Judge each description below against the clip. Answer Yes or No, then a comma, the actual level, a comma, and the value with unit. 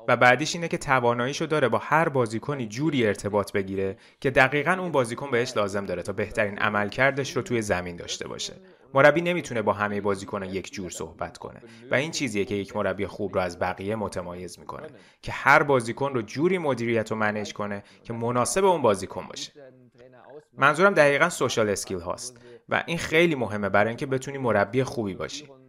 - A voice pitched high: No, low, 120 Hz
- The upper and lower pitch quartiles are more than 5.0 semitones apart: Yes, wide, 5.4 semitones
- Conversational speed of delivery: No, fast, 180 wpm